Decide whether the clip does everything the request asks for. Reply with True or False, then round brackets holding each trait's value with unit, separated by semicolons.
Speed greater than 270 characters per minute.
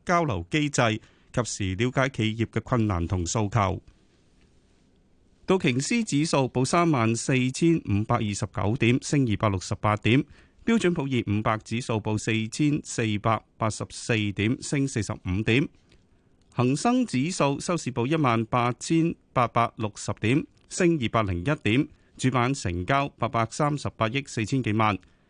False (230 characters per minute)